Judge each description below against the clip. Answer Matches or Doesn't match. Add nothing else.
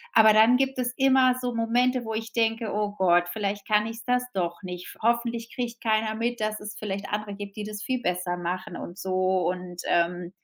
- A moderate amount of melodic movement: Matches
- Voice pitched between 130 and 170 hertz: Doesn't match